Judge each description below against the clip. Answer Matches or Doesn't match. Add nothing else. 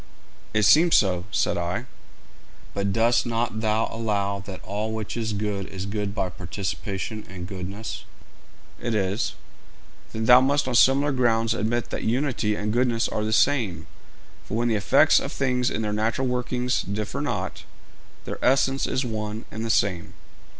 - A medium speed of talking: Matches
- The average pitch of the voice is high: Doesn't match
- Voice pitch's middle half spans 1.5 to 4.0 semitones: Matches